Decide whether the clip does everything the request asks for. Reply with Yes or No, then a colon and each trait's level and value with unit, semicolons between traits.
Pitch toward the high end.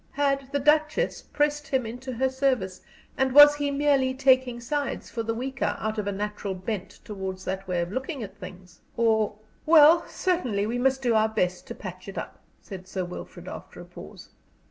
Yes: high, 245 Hz